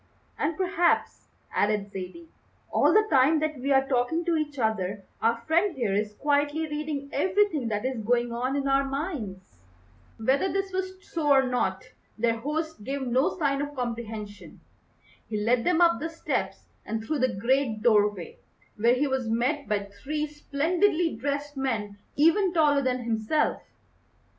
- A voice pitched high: Yes, very high, 270 Hz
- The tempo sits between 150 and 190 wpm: Yes, average, 160 wpm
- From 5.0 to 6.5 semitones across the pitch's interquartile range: Yes, wide, 5.5 semitones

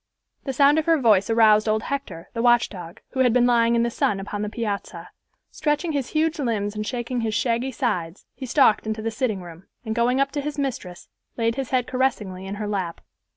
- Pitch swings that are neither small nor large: Yes, average, 4.1 semitones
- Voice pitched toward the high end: Yes, high, 230 Hz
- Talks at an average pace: No, fast, 215 wpm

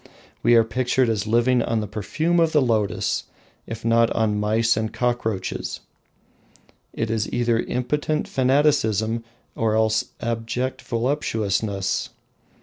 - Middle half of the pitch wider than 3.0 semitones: No, narrow, 2.4 semitones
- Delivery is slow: Yes, slow, 125 wpm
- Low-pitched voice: Yes, low, 115 Hz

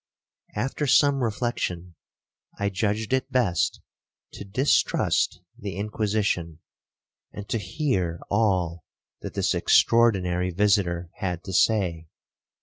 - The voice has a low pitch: Yes, low, 100 Hz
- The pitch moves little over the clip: No, average, 4.3 semitones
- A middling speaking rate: No, slow, 105 wpm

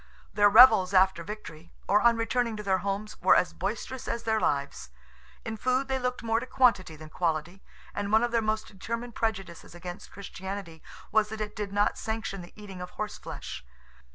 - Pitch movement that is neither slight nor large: Yes, average, 3.4 semitones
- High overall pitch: Yes, high, 210 Hz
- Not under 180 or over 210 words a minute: Yes, average, 190 wpm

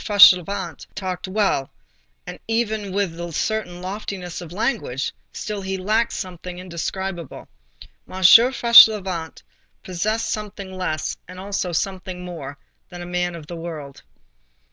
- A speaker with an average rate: No, slow, 120 wpm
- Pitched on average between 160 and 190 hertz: Yes, medium, 185 Hz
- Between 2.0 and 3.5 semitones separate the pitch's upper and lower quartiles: Yes, average, 2.8 semitones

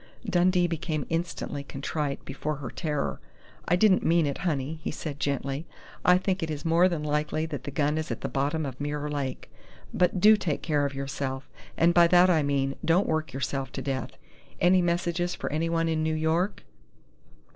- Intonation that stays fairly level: No, average, 3.3 semitones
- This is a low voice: No, medium, 155 Hz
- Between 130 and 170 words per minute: No, average, 190 wpm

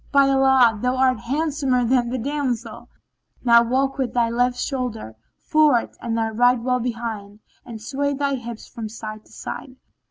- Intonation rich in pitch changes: No, narrow, 2.6 semitones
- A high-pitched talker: Yes, high, 245 Hz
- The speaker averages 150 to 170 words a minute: Yes, average, 165 wpm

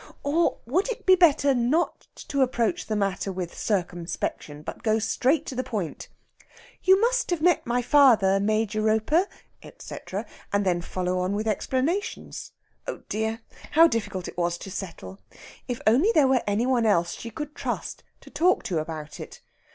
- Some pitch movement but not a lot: No, wide, 6.9 semitones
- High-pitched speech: Yes, high, 225 Hz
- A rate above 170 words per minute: No, average, 165 wpm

